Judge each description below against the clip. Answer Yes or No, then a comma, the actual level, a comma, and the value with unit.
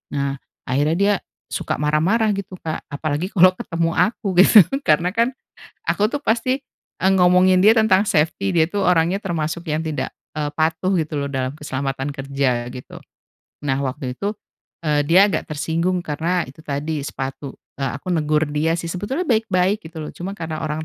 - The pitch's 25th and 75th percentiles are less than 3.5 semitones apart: No, average, 4.3 semitones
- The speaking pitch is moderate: Yes, medium, 160 Hz